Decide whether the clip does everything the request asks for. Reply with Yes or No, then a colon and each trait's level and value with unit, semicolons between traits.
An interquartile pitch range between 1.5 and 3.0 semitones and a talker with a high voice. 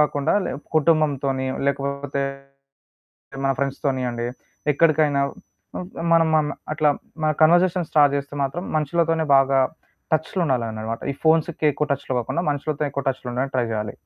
No: narrow, 2.6 semitones; medium, 145 Hz